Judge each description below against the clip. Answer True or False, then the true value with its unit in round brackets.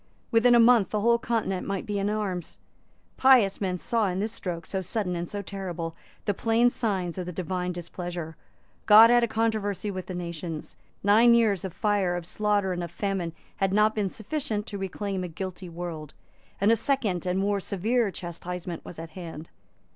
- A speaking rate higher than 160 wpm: True (190 wpm)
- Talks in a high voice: True (195 Hz)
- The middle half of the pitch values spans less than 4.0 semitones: True (3.4 semitones)